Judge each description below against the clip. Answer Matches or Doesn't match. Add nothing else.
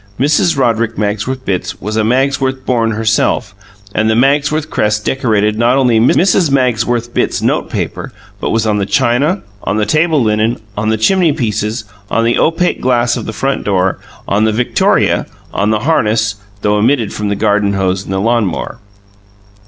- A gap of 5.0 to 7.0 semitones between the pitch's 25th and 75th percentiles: Doesn't match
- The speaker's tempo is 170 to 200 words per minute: Matches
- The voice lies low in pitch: Matches